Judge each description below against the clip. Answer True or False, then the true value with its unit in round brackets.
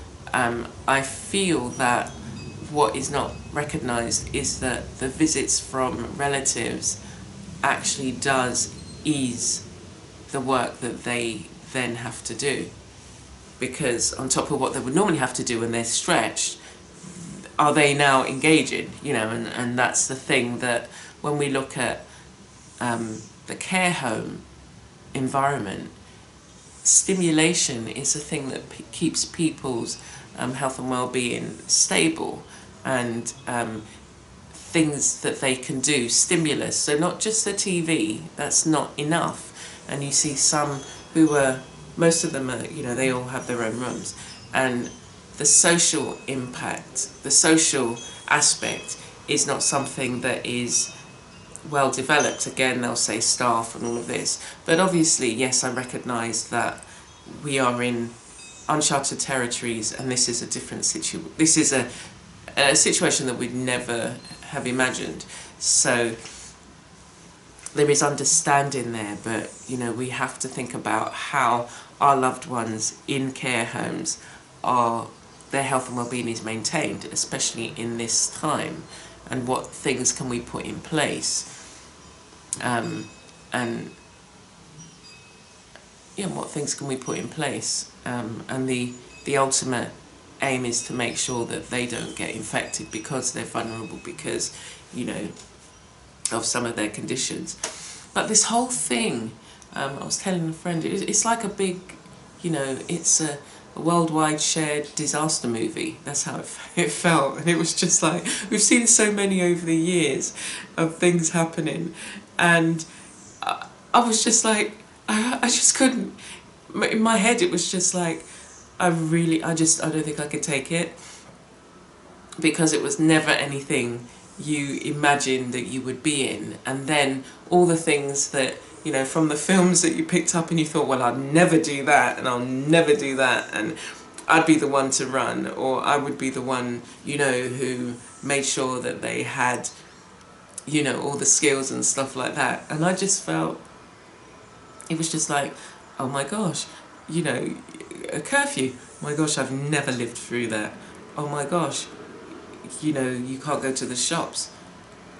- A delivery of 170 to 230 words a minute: False (155 wpm)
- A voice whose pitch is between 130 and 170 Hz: True (135 Hz)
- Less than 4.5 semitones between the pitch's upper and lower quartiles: False (4.8 semitones)